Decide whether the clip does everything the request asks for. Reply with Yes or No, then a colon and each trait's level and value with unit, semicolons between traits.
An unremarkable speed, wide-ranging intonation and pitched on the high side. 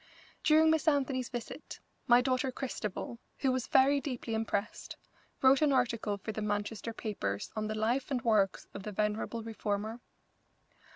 No: average, 155 wpm; average, 3.7 semitones; high, 230 Hz